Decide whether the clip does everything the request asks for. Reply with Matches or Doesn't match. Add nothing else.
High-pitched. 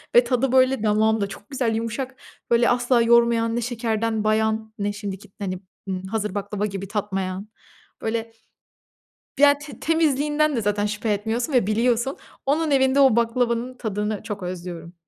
Matches